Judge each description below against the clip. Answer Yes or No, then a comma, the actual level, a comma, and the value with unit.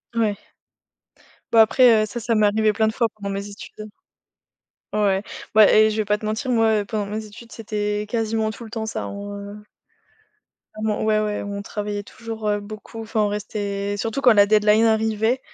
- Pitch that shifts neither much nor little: No, narrow, 1.2 semitones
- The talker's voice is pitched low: No, high, 215 Hz